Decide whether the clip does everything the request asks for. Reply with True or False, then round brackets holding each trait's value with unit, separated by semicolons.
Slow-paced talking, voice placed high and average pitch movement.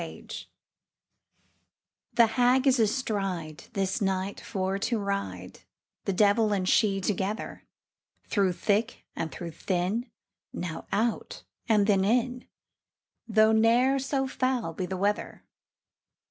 True (120 wpm; 205 Hz; 3.5 semitones)